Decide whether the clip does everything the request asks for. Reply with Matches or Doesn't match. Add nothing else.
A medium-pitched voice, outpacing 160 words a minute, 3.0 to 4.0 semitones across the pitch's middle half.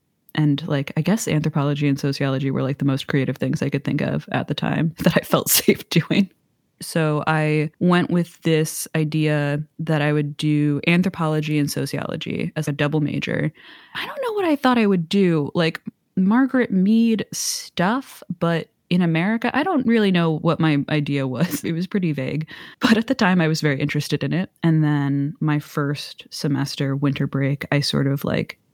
Matches